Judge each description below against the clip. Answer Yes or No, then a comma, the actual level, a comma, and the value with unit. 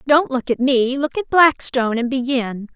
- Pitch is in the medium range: No, very high, 260 Hz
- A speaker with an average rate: Yes, average, 175 wpm